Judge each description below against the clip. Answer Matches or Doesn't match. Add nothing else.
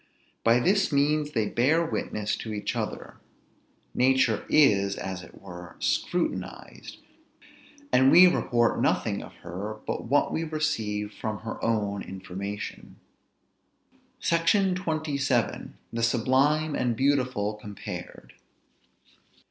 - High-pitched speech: Doesn't match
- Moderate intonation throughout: Doesn't match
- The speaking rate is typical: Doesn't match